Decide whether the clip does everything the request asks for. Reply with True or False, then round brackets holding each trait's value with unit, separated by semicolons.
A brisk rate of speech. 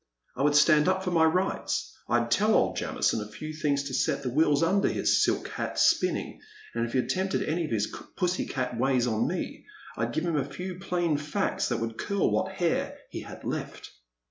True (220 wpm)